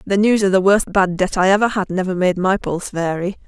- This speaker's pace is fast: Yes, fast, 260 wpm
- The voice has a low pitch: No, high, 190 Hz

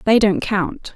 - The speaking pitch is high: Yes, high, 210 Hz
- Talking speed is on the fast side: No, average, 190 wpm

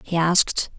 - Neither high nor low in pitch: Yes, medium, 170 Hz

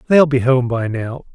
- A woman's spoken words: No, male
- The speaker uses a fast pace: Yes, fast, 225 wpm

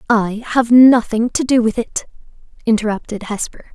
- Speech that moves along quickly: No, average, 145 wpm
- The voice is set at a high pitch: Yes, high, 230 Hz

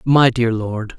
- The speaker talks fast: No, average, 185 wpm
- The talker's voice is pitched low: Yes, low, 120 Hz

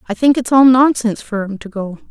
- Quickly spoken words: Yes, fast, 255 wpm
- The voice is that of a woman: Yes, female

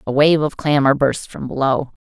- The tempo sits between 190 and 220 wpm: Yes, fast, 205 wpm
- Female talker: Yes, female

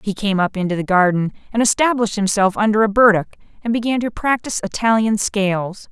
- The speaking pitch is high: Yes, high, 210 Hz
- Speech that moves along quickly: No, average, 185 wpm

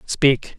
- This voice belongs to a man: Yes, male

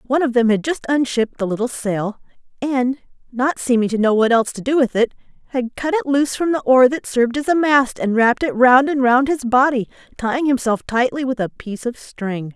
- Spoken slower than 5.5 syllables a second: No, 5.7 syllables/s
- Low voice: No, very high, 250 Hz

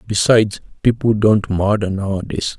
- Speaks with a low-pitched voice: Yes, low, 105 Hz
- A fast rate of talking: No, slow, 115 wpm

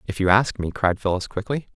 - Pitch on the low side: Yes, low, 105 Hz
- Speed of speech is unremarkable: No, fast, 240 wpm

